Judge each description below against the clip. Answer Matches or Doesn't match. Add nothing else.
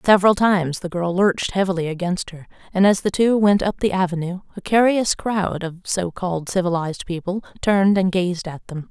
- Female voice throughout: Matches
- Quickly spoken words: Doesn't match